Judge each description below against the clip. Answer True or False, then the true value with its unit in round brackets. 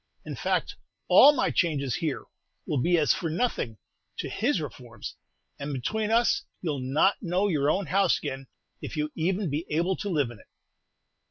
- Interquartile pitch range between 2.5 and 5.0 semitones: False (5.5 semitones)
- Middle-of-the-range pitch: True (160 Hz)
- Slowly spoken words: False (180 wpm)